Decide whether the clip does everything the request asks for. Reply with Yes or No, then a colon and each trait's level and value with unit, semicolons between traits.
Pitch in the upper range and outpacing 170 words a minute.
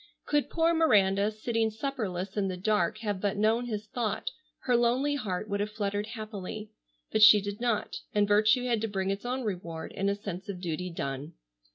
Yes: high, 210 Hz; average, 195 wpm